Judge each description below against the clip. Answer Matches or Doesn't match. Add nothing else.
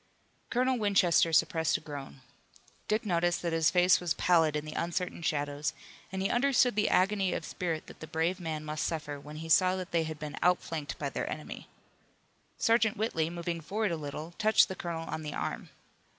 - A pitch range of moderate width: Matches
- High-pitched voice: Doesn't match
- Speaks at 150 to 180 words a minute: Doesn't match